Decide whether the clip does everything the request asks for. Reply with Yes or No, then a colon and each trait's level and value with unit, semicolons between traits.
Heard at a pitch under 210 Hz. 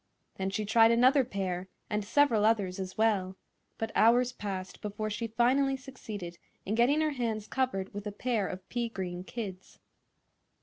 No: high, 215 Hz